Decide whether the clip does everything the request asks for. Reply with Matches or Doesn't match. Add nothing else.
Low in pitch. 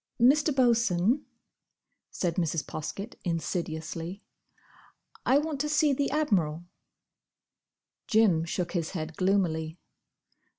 Doesn't match